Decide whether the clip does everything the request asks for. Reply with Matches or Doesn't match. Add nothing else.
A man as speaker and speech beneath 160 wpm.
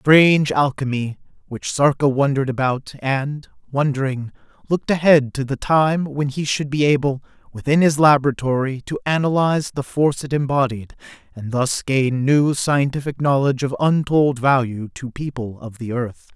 Matches